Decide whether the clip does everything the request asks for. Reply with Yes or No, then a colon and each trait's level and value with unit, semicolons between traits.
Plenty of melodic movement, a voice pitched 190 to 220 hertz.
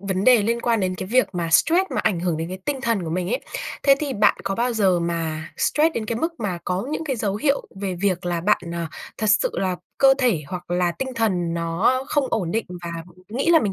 Yes: wide, 5.9 semitones; high, 200 Hz